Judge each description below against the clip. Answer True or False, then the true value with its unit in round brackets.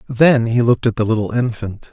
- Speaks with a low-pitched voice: True (115 Hz)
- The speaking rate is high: True (220 wpm)